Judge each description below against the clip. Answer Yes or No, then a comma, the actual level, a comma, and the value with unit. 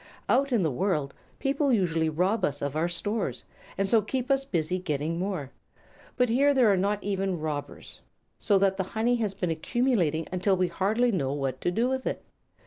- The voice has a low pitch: No, high, 190 Hz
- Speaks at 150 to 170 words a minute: No, average, 195 wpm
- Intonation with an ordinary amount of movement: No, wide, 6.1 semitones